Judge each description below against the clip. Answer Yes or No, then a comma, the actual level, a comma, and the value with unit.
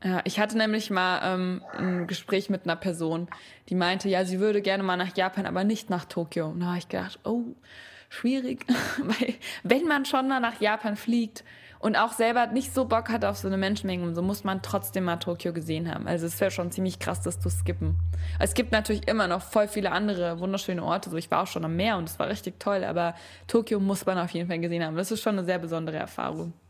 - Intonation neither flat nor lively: Yes, average, 4.0 semitones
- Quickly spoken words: Yes, fast, 235 wpm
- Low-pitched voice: No, medium, 185 Hz